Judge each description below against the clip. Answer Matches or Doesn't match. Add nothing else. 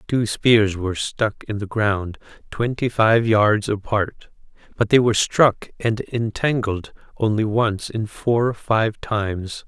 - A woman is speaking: Doesn't match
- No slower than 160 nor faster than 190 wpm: Doesn't match